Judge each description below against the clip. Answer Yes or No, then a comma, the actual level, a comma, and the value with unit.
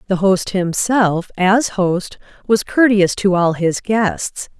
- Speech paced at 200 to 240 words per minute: No, average, 145 wpm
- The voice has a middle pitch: No, high, 195 Hz